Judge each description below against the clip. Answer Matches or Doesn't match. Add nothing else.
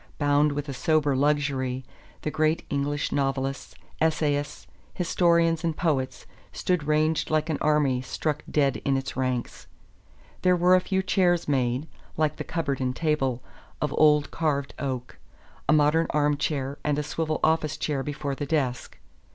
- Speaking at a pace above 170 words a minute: Doesn't match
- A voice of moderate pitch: Matches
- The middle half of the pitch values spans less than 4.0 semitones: Matches